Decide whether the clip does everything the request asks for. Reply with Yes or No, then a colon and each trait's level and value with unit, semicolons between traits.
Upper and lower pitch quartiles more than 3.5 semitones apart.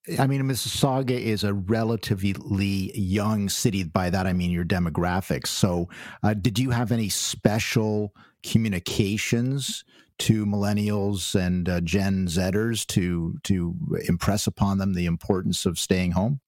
No: average, 2.9 semitones